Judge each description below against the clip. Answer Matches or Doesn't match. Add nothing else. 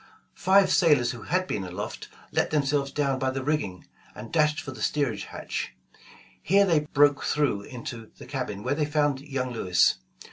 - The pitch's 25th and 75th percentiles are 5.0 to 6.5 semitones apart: Doesn't match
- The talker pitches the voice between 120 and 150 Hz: Matches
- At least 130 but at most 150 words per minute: Doesn't match